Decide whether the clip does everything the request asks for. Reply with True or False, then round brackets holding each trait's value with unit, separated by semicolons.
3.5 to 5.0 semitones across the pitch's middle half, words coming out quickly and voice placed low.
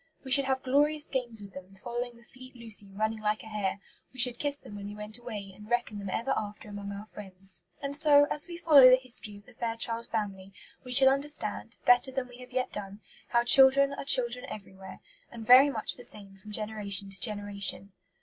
False (4.1 semitones; 215 wpm; 230 Hz)